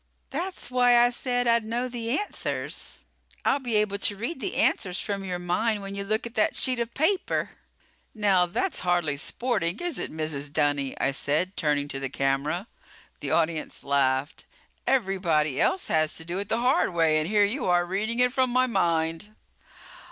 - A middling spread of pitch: No, wide, 6.9 semitones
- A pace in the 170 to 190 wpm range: Yes, average, 185 wpm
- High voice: Yes, high, 195 Hz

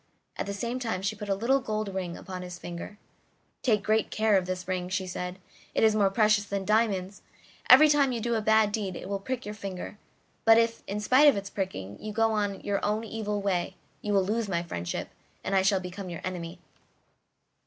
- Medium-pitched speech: No, high, 205 Hz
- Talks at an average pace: No, fast, 220 wpm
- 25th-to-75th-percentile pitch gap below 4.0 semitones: Yes, average, 2.8 semitones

